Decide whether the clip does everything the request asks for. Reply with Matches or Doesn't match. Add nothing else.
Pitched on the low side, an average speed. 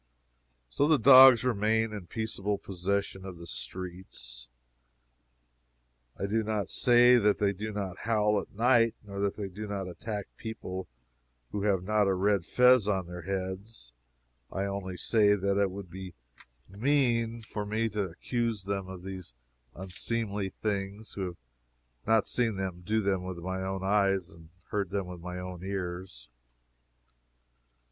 Matches